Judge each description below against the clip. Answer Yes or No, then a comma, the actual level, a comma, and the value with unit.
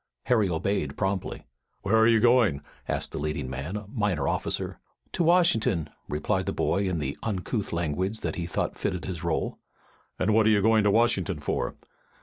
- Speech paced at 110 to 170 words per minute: No, average, 180 wpm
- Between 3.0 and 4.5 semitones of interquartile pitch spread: No, average, 5.1 semitones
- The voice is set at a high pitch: No, low, 100 Hz